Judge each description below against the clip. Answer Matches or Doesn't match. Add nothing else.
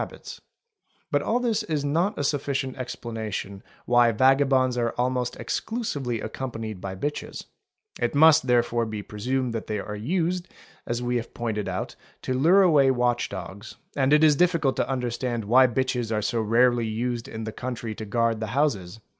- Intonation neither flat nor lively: Matches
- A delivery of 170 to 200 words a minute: Matches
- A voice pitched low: Matches